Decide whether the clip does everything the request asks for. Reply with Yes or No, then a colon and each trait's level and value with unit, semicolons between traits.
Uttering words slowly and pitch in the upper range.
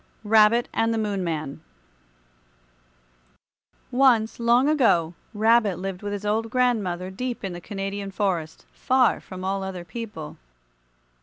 Yes: slow, 130 wpm; high, 205 Hz